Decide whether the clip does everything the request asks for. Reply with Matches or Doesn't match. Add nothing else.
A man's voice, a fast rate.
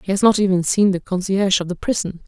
Doesn't match